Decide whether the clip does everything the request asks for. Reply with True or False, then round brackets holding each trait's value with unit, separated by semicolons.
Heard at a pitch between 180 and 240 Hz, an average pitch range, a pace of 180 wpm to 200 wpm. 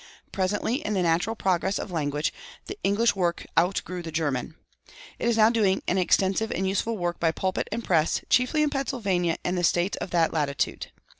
True (185 Hz; 4.1 semitones; 190 wpm)